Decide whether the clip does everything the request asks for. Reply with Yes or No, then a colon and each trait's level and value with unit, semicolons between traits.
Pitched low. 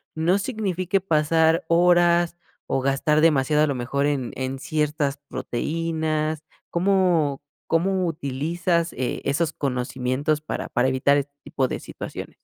No: medium, 155 Hz